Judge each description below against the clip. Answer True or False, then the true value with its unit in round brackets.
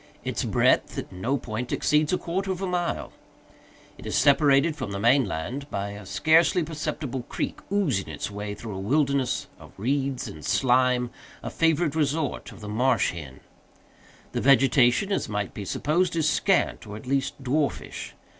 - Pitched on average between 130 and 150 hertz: True (135 Hz)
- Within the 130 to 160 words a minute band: False (170 wpm)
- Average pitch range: False (6.1 semitones)